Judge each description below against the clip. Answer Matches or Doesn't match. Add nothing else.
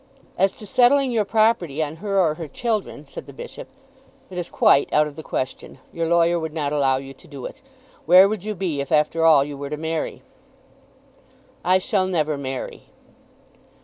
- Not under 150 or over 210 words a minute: Matches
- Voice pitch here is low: Doesn't match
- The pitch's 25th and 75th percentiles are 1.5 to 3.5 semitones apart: Doesn't match